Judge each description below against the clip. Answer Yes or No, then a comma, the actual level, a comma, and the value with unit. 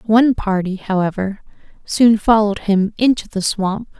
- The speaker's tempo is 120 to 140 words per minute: Yes, slow, 135 wpm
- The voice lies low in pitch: No, high, 210 Hz